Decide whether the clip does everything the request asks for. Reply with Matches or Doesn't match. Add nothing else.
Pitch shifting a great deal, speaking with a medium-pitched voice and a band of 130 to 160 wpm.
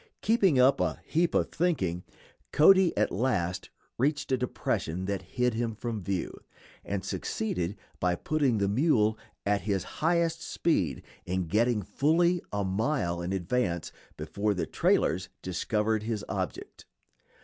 Doesn't match